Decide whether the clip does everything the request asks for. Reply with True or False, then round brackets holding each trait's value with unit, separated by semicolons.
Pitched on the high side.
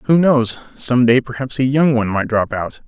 False (125 Hz)